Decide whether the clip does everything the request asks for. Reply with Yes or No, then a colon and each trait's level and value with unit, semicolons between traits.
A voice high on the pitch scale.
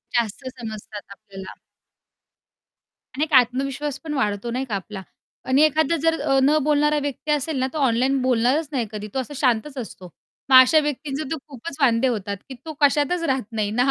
Yes: very high, 260 Hz